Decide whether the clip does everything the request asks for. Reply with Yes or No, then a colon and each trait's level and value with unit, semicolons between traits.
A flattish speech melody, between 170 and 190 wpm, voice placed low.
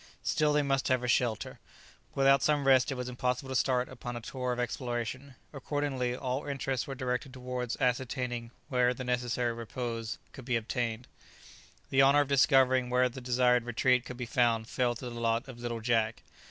Yes: narrow, 1.6 semitones; average, 185 wpm; low, 125 Hz